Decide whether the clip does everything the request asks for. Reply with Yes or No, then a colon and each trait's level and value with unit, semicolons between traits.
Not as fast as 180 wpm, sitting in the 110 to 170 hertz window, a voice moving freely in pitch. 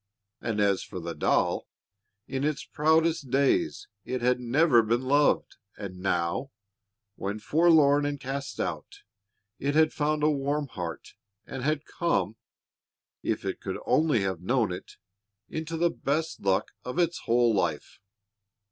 Yes: average, 145 wpm; low, 135 Hz; wide, 6.4 semitones